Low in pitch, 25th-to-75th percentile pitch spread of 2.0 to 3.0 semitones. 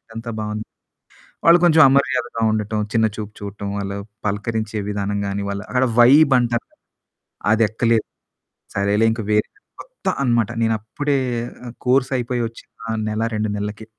Yes: low, 110 Hz; average, 2.7 semitones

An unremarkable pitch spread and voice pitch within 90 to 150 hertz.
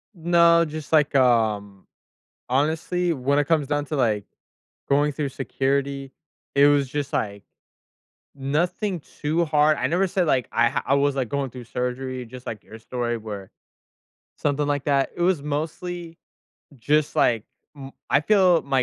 Yes: average, 3.6 semitones; medium, 140 Hz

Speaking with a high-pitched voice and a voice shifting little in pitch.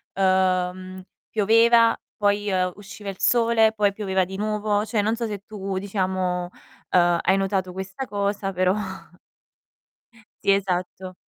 Yes: high, 195 Hz; narrow, 2.1 semitones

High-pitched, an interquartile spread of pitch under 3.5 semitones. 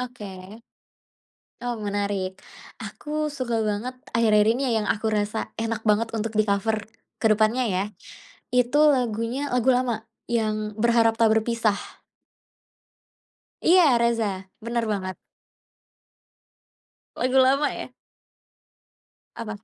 Yes: high, 225 Hz; narrow, 2.5 semitones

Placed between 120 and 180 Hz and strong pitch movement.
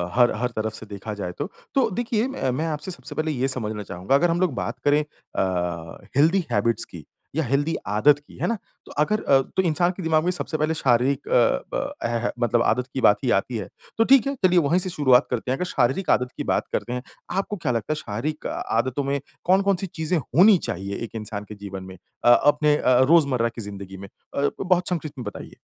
Yes: low, 135 Hz; wide, 6.7 semitones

